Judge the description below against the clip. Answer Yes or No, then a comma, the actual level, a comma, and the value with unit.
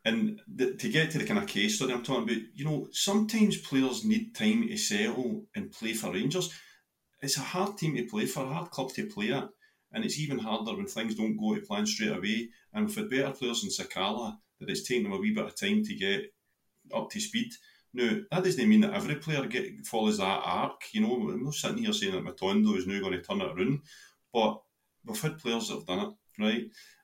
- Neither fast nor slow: No, fast, 225 wpm